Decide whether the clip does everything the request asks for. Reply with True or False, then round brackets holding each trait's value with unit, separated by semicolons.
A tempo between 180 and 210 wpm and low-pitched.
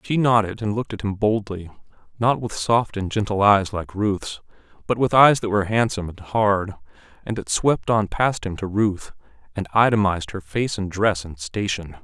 True (195 wpm; 100 Hz)